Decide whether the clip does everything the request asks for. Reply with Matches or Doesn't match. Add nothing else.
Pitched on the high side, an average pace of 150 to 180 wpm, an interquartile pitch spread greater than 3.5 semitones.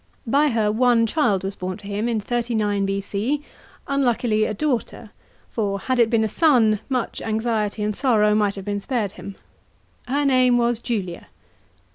Doesn't match